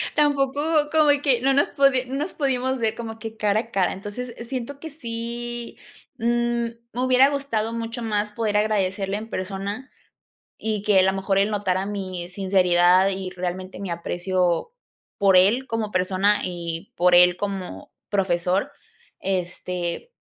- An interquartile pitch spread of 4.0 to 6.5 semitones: Yes, average, 4.4 semitones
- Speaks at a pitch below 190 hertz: No, high, 205 Hz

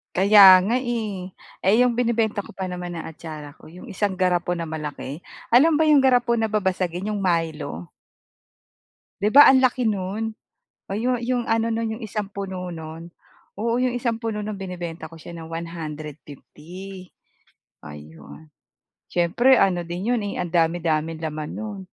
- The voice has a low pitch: No, medium, 185 Hz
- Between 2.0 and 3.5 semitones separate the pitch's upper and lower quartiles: No, average, 5.0 semitones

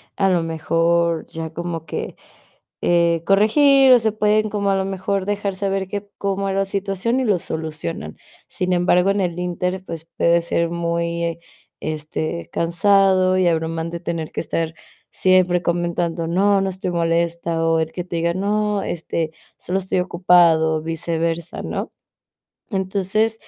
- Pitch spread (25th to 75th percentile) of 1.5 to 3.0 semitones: Yes, average, 2.7 semitones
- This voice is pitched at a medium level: Yes, medium, 175 Hz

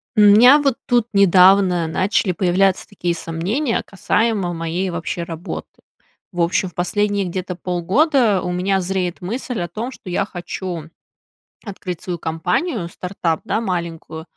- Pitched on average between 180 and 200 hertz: Yes, medium, 185 Hz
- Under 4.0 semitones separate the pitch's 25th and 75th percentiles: Yes, average, 3.1 semitones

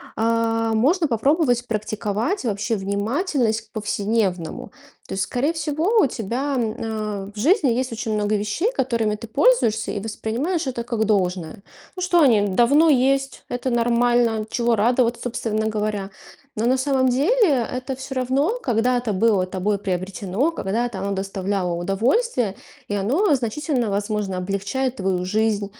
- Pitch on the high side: Yes, high, 230 Hz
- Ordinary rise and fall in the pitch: Yes, average, 4.2 semitones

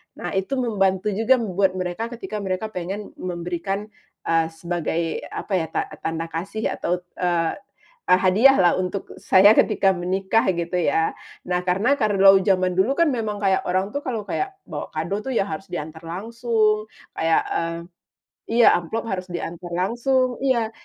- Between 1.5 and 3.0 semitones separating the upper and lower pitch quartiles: No, average, 3.9 semitones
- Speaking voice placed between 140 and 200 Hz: Yes, high, 190 Hz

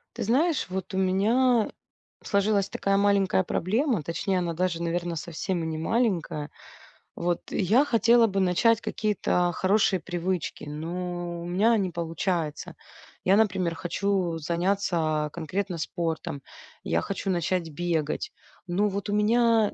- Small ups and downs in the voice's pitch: No, average, 3.3 semitones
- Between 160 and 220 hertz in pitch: Yes, medium, 185 Hz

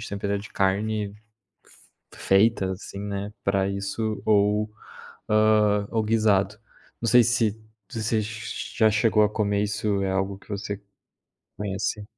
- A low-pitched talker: Yes, low, 105 Hz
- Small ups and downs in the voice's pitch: Yes, narrow, 1.5 semitones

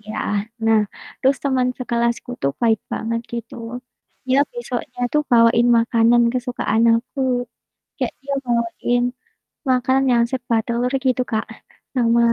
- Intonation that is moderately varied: No, narrow, 1.7 semitones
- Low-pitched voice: No, high, 240 Hz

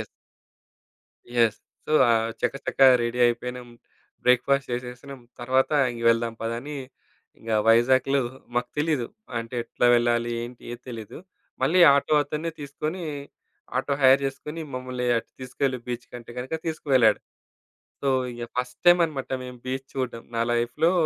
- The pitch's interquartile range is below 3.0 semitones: Yes, narrow, 2.6 semitones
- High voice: No, low, 125 Hz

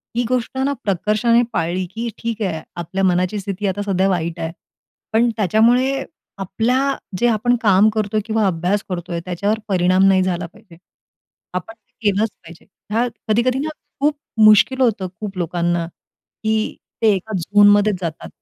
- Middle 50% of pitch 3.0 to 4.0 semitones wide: Yes, average, 3.6 semitones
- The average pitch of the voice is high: Yes, high, 205 Hz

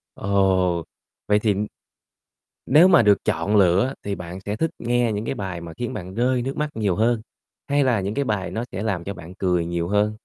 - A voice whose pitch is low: Yes, low, 105 Hz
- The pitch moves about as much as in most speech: Yes, average, 4.4 semitones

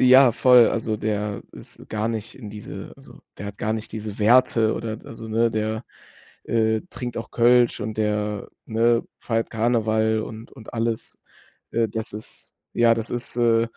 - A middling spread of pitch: No, narrow, 1.4 semitones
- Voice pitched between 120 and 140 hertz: No, low, 110 Hz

